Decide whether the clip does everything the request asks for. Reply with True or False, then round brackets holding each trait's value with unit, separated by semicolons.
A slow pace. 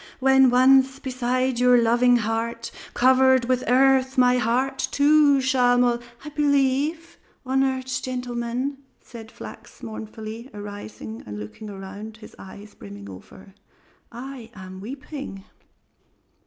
True (120 wpm)